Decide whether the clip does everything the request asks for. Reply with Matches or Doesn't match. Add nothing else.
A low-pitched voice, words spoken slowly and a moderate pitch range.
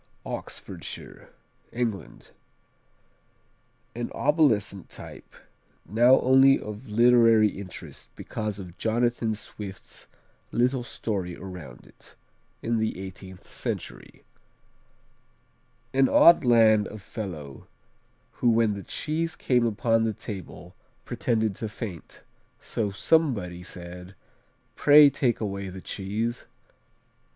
Matches